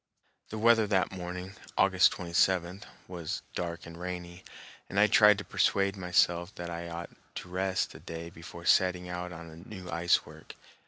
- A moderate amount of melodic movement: No, narrow, 1.8 semitones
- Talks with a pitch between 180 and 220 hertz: No, very low, 90 Hz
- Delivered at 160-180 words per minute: Yes, average, 165 wpm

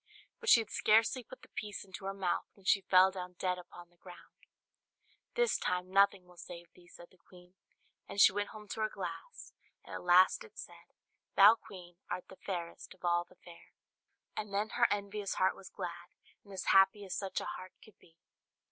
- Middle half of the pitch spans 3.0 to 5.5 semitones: No, narrow, 2.4 semitones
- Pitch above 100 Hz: Yes, high, 190 Hz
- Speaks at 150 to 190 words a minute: No, fast, 205 wpm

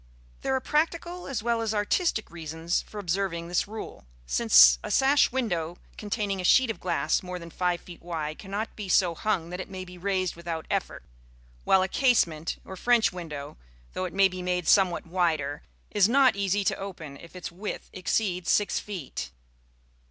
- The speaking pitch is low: No, medium, 185 Hz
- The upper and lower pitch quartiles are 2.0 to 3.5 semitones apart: No, average, 3.9 semitones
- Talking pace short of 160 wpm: No, average, 180 wpm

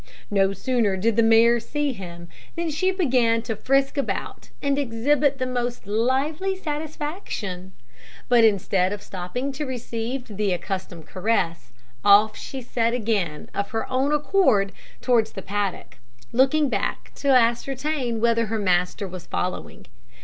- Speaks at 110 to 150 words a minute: Yes, average, 140 wpm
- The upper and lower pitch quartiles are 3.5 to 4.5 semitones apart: No, average, 5.2 semitones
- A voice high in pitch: Yes, high, 230 Hz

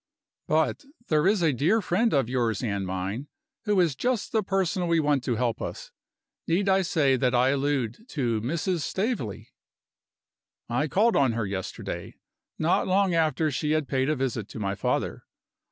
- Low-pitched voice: No, medium, 145 Hz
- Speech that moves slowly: No, average, 170 wpm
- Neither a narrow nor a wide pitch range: No, wide, 6.9 semitones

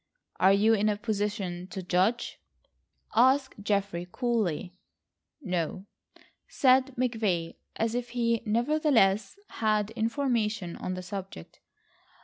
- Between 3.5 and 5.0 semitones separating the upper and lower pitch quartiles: Yes, average, 4.0 semitones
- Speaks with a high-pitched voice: Yes, high, 210 Hz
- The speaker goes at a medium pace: No, slow, 110 wpm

